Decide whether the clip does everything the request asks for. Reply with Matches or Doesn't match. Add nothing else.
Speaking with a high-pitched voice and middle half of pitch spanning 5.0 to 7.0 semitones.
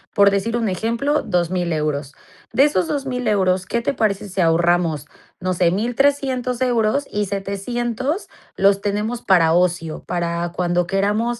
Matches